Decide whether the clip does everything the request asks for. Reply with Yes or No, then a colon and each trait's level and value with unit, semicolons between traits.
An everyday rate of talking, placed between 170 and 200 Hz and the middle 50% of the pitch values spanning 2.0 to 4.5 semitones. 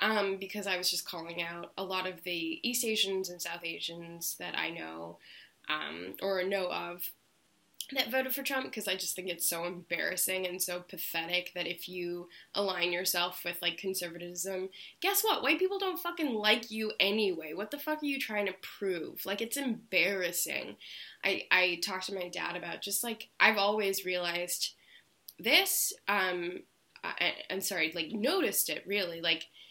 Yes: average, 175 wpm; medium, 185 Hz; average, 3.5 semitones